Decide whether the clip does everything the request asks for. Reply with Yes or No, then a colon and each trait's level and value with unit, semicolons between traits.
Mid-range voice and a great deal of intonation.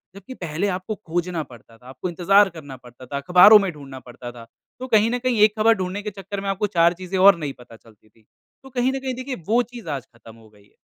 Yes: medium, 180 Hz; wide, 8.0 semitones